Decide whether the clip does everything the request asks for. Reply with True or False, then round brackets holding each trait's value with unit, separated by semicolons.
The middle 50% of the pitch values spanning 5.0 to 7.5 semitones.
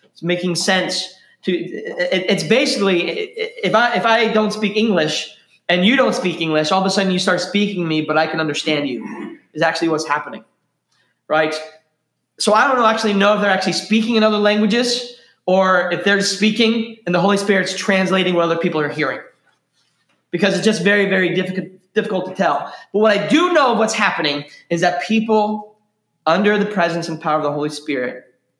False (4.0 semitones)